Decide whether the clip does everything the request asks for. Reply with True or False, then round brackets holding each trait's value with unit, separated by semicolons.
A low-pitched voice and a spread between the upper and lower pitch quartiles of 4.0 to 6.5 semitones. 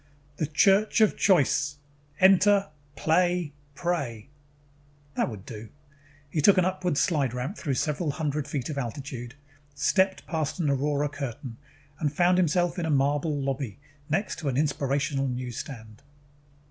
False (145 Hz; 4.4 semitones)